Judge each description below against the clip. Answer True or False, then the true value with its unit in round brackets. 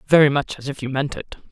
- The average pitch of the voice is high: False (140 Hz)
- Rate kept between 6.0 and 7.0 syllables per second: True (6.4 syllables/s)